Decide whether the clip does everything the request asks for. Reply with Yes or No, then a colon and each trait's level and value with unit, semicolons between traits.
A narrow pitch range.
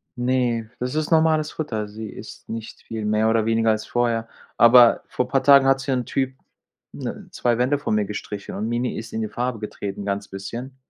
No: average, 3.1 semitones